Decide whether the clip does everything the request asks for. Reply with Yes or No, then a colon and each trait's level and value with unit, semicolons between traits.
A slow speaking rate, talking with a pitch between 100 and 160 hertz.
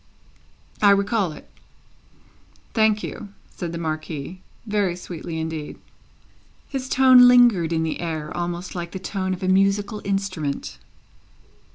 No: slow, 130 wpm; medium, 185 Hz